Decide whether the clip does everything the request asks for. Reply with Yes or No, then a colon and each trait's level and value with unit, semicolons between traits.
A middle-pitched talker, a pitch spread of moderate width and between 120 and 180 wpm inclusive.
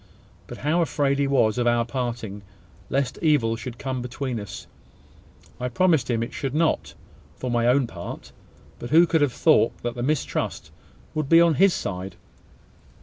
No: low, 130 Hz; average, 3.9 semitones; average, 170 wpm